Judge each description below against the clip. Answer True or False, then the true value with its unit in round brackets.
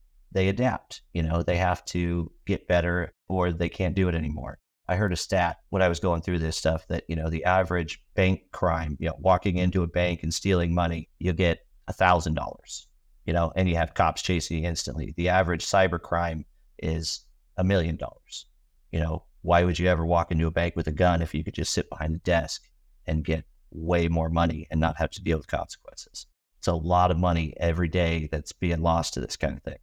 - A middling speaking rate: False (225 wpm)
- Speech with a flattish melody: True (1.9 semitones)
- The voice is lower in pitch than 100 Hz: True (85 Hz)